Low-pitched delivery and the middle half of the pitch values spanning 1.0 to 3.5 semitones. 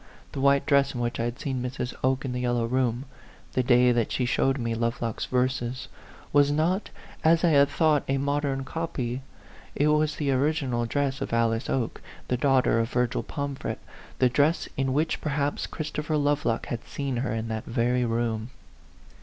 Yes: low, 130 Hz; average, 3.0 semitones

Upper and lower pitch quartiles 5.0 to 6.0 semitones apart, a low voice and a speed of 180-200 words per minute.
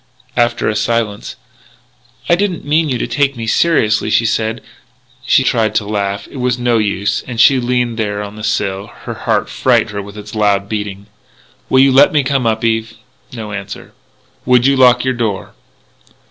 No: average, 3.4 semitones; low, 115 Hz; average, 190 wpm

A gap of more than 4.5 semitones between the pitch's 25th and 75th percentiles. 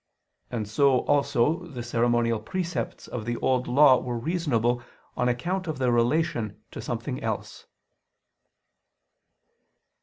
No: average, 4.1 semitones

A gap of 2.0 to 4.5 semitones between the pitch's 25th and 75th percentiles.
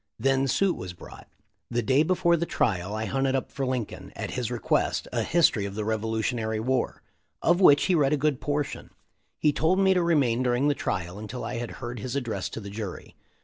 No: average, 5.1 semitones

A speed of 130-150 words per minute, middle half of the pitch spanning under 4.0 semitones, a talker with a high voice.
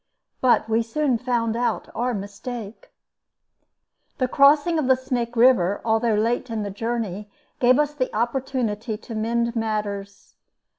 Yes: average, 140 wpm; average, 2.8 semitones; high, 235 Hz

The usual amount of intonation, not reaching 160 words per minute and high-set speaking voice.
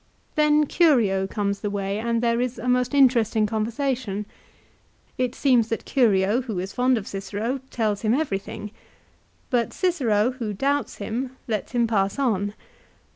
Yes: average, 3.7 semitones; average, 150 wpm; high, 230 Hz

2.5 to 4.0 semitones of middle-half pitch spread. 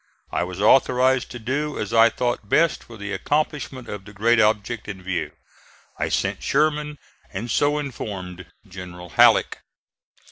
No: average, 5.3 semitones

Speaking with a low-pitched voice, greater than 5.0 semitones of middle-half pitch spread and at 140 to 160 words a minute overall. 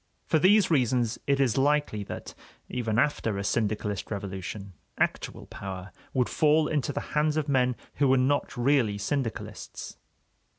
Yes: low, 125 Hz; wide, 5.5 semitones; average, 145 wpm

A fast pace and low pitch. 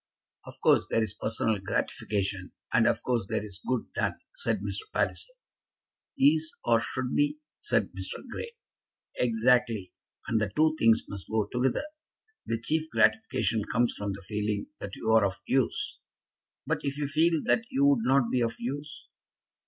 No: average, 165 wpm; low, 120 Hz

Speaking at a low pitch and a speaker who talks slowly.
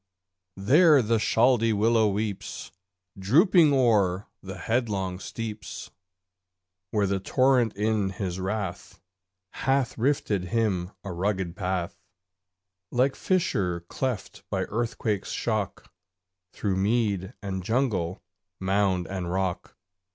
Yes: low, 105 Hz; slow, 105 wpm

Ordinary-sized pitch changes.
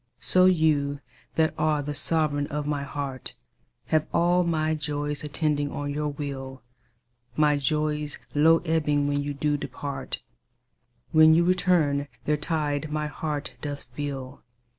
No: narrow, 1.6 semitones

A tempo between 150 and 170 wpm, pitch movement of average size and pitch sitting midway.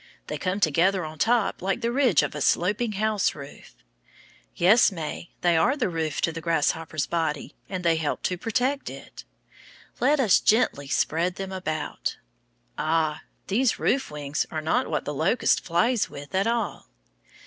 No: average, 165 wpm; wide, 5.7 semitones; medium, 180 Hz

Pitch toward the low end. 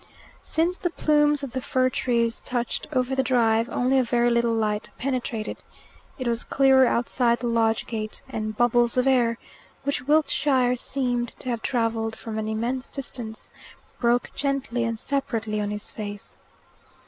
No: high, 240 Hz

